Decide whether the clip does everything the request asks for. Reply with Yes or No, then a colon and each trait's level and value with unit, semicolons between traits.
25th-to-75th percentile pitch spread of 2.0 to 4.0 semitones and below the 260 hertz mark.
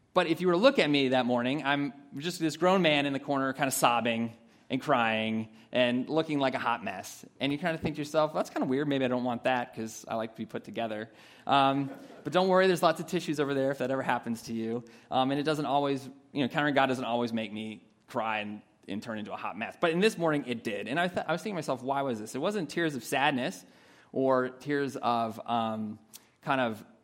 No: average, 4.8 semitones; low, 135 Hz